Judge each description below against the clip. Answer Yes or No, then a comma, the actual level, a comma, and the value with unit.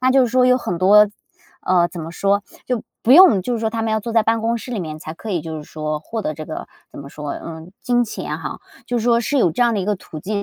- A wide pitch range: Yes, wide, 6.1 semitones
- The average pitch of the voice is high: Yes, high, 210 Hz